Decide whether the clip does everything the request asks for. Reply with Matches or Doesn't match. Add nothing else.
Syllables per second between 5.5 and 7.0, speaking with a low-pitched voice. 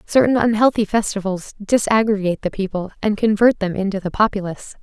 Doesn't match